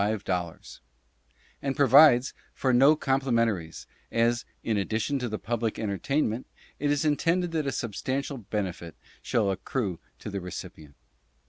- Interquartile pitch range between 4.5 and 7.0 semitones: Yes, wide, 5.4 semitones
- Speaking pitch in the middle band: No, low, 115 Hz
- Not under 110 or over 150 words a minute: Yes, slow, 135 wpm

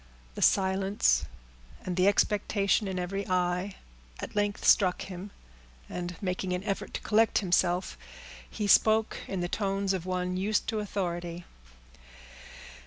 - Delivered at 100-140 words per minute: Yes, slow, 135 wpm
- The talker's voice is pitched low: No, high, 190 Hz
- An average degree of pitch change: No, narrow, 2.1 semitones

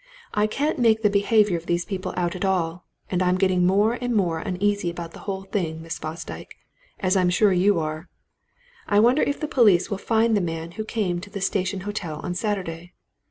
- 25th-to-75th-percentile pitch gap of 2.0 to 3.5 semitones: Yes, average, 3.2 semitones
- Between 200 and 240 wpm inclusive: Yes, fast, 205 wpm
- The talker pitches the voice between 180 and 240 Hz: Yes, high, 190 Hz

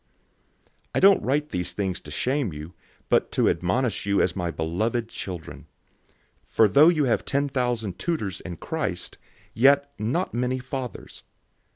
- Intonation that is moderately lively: No, wide, 7.1 semitones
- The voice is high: No, low, 120 Hz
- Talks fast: No, average, 160 wpm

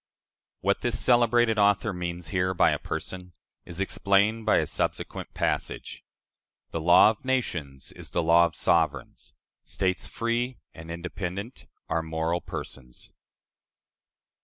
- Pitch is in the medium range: No, very low, 90 Hz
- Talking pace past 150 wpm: No, slow, 135 wpm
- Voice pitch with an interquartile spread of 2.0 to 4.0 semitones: No, average, 4.6 semitones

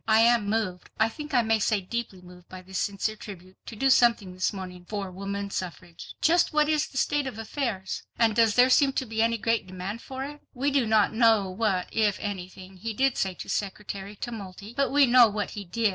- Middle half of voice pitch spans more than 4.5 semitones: No, average, 3.8 semitones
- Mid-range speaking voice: No, high, 215 Hz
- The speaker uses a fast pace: Yes, fast, 220 wpm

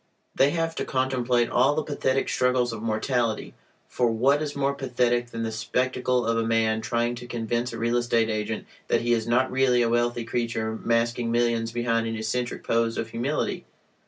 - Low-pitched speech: Yes, low, 120 Hz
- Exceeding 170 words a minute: Yes, average, 190 wpm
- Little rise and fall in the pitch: Yes, narrow, 1.7 semitones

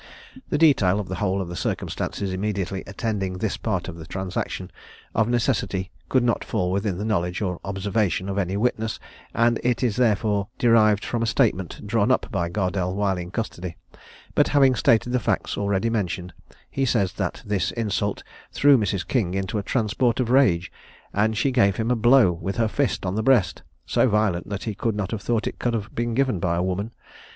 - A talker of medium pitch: No, low, 105 Hz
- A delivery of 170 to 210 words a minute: Yes, average, 200 wpm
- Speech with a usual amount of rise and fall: Yes, average, 3.6 semitones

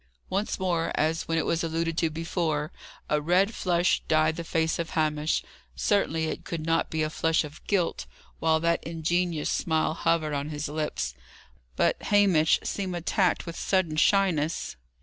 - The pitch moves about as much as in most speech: No, narrow, 1.9 semitones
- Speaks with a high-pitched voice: No, medium, 165 Hz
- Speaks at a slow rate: No, average, 165 wpm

